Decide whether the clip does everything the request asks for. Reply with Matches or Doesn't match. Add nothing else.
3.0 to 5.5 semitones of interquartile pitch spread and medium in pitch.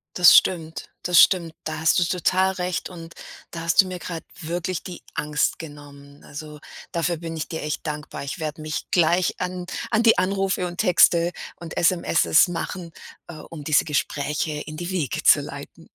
Doesn't match